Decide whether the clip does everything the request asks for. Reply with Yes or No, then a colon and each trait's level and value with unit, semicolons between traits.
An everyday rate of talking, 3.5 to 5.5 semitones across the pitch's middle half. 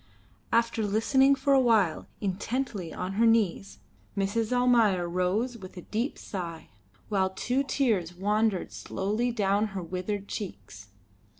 No: slow, 130 wpm; average, 4.0 semitones